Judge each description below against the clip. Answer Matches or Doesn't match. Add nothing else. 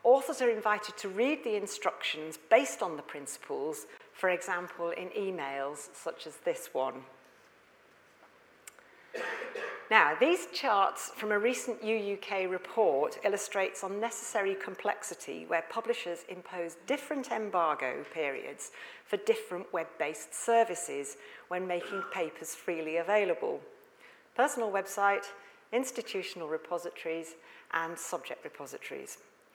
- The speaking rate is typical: Doesn't match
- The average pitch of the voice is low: Doesn't match